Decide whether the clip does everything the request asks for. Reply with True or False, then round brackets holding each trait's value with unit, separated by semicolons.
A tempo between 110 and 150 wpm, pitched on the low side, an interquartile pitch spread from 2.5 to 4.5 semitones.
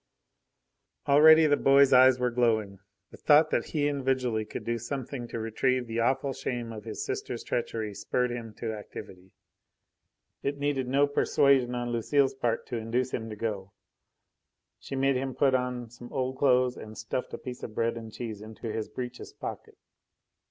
False (175 wpm; 125 Hz; 2.9 semitones)